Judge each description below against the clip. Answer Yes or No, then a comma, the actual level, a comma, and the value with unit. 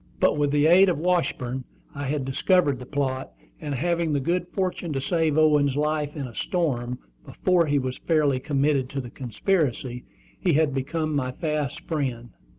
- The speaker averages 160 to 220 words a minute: Yes, average, 175 wpm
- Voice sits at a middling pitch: Yes, medium, 145 Hz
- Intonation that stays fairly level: No, average, 3.5 semitones